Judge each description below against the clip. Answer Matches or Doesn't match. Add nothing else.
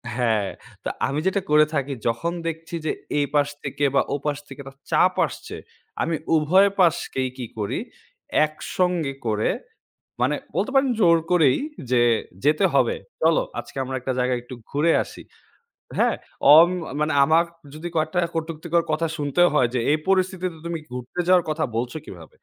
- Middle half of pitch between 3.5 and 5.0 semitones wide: Matches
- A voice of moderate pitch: Matches